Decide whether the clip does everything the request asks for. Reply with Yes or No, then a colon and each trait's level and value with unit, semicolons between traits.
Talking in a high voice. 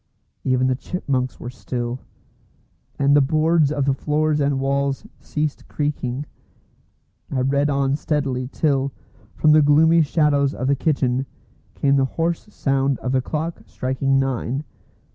No: medium, 140 Hz